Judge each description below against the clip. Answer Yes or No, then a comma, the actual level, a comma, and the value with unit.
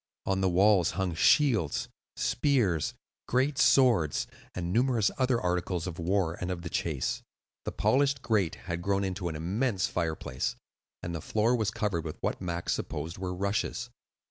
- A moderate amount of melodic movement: Yes, average, 4.9 semitones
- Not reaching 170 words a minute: Yes, average, 160 wpm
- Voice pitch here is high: No, very low, 95 Hz